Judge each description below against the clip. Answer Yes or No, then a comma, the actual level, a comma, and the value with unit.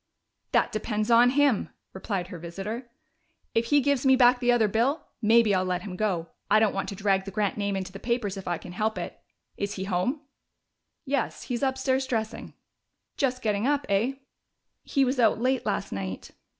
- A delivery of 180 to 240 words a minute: Yes, average, 190 wpm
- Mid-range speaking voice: No, high, 220 Hz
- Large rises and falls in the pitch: No, average, 4.5 semitones